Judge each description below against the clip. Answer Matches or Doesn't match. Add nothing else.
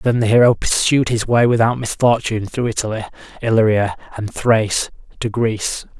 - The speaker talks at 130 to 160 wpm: Matches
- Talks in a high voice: Doesn't match